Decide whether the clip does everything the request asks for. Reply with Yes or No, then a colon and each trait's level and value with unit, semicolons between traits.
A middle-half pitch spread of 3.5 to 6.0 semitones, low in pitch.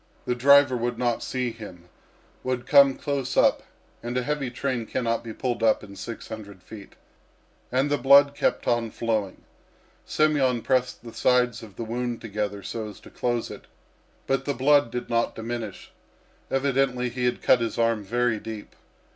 No: narrow, 2.5 semitones; low, 120 Hz